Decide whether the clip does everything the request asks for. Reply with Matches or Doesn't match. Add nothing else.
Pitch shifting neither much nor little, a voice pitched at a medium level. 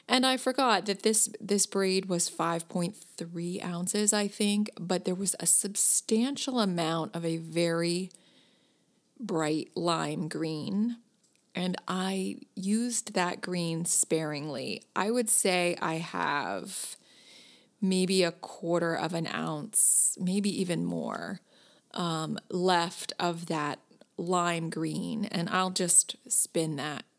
Matches